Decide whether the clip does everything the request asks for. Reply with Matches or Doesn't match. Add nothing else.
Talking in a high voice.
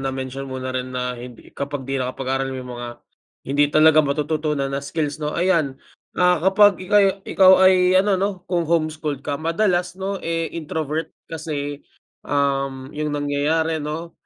Doesn't match